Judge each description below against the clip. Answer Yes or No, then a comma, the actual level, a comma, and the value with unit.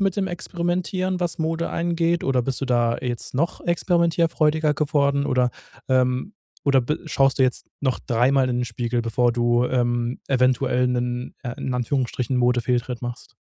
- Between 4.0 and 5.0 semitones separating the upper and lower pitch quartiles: Yes, average, 4.7 semitones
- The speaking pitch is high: No, low, 130 Hz